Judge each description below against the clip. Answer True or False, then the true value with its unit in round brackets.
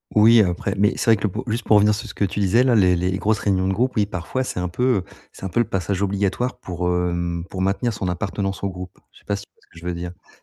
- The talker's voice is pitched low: True (95 Hz)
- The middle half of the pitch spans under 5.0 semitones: True (2.8 semitones)